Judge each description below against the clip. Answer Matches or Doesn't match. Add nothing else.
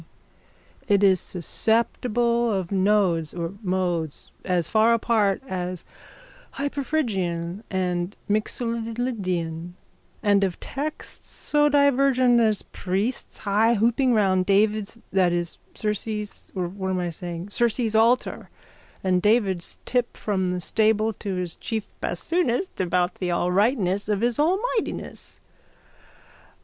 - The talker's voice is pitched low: Doesn't match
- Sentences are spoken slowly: Matches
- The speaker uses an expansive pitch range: Doesn't match